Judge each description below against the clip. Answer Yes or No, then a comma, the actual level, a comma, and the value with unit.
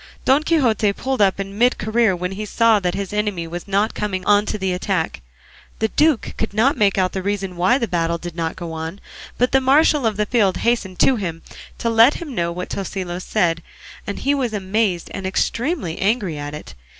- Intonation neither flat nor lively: Yes, average, 4.1 semitones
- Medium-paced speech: No, fast, 210 wpm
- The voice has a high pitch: Yes, high, 200 Hz